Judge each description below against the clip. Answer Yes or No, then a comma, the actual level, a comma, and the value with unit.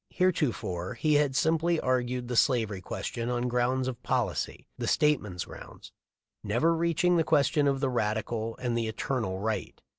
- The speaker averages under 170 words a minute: No, average, 175 wpm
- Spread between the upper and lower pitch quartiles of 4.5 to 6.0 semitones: Yes, average, 5.1 semitones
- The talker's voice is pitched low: Yes, low, 125 Hz